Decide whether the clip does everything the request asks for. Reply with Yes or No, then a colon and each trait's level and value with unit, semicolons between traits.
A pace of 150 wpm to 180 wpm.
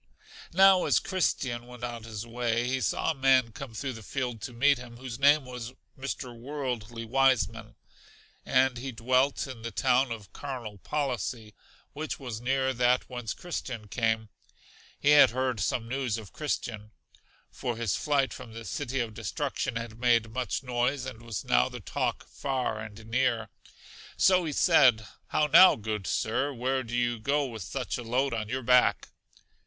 Yes: average, 170 wpm